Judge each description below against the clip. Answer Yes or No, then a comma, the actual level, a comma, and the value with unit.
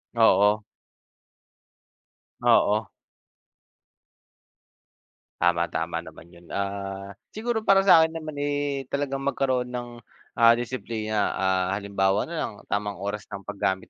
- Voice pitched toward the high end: No, low, 110 Hz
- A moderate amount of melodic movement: No, wide, 6.0 semitones